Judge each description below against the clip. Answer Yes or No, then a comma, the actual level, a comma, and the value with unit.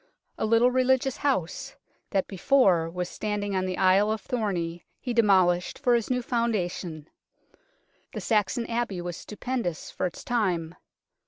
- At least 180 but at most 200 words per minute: No, average, 150 wpm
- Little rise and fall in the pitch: No, average, 5.1 semitones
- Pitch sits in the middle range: No, high, 205 Hz